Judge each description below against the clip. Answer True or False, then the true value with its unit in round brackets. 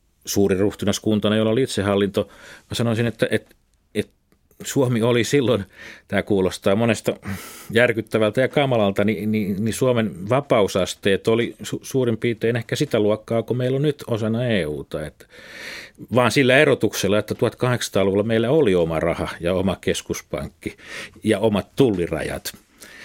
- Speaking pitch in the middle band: False (110 Hz)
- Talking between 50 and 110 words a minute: False (140 wpm)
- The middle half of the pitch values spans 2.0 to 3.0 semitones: True (2.6 semitones)